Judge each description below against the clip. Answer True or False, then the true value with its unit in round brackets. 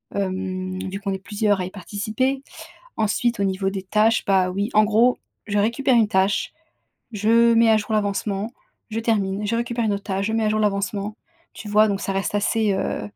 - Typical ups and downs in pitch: False (2.3 semitones)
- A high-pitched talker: True (205 Hz)